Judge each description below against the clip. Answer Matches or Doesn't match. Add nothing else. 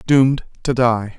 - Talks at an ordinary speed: Matches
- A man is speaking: Matches